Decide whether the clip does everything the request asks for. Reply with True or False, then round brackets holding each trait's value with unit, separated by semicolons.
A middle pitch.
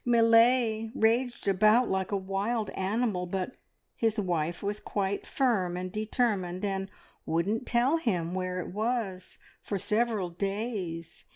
False (205 Hz)